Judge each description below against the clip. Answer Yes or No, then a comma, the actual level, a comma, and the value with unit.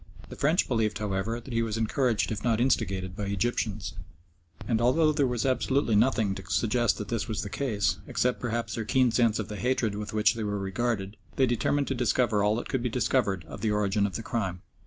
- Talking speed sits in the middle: No, fast, 220 wpm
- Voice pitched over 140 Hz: No, low, 115 Hz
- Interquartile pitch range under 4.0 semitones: Yes, average, 3.1 semitones